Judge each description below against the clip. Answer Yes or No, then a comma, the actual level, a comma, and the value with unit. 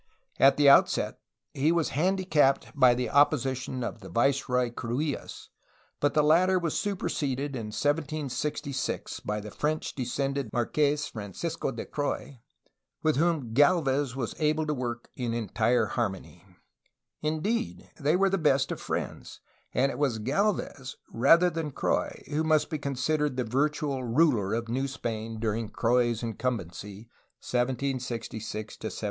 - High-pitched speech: No, low, 135 Hz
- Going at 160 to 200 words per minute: No, average, 140 wpm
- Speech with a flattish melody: No, average, 4.3 semitones